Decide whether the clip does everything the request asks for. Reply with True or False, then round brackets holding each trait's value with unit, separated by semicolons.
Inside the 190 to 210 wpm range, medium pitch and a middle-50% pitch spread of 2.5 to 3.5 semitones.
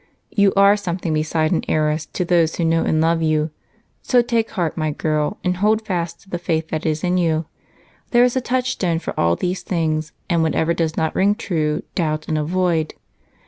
True (200 wpm; 165 Hz; 3.1 semitones)